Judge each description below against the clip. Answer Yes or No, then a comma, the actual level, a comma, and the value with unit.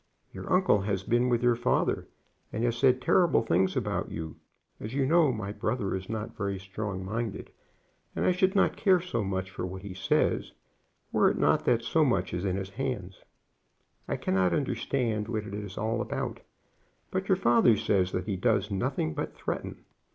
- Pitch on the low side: Yes, low, 110 Hz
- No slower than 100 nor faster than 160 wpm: No, average, 190 wpm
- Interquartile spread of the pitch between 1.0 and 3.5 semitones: No, average, 4.4 semitones